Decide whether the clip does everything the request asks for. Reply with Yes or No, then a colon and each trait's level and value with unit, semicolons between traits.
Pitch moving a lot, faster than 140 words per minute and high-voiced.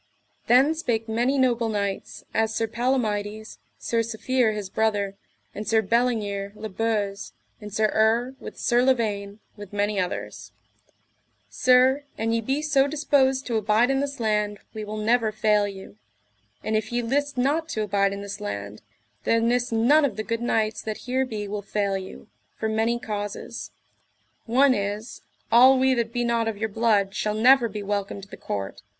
No: average, 3.0 semitones; average, 175 wpm; high, 220 Hz